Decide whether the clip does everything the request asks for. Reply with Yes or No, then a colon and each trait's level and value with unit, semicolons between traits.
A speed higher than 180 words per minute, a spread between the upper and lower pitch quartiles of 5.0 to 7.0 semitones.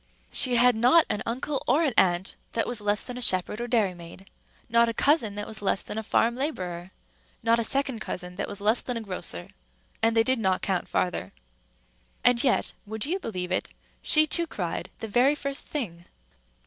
No: average, 200 wpm; average, 4.6 semitones